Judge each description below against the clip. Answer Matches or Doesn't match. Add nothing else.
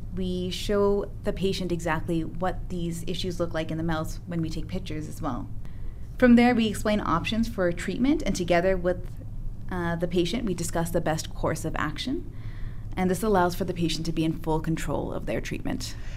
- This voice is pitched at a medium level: Matches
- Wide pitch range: Matches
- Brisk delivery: Doesn't match